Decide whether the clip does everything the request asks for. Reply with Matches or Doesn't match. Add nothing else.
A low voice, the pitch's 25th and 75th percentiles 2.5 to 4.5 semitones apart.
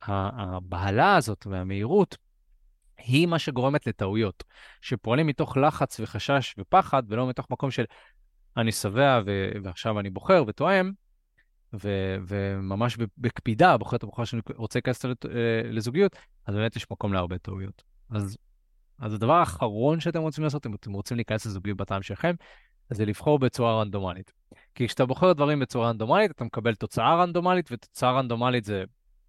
Doesn't match